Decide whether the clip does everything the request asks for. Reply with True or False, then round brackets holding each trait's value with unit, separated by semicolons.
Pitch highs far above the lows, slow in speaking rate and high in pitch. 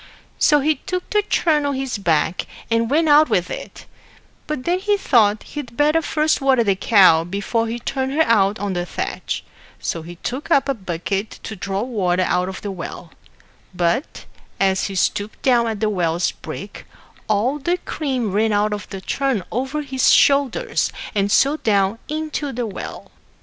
False (6.5 semitones; 180 wpm; 230 Hz)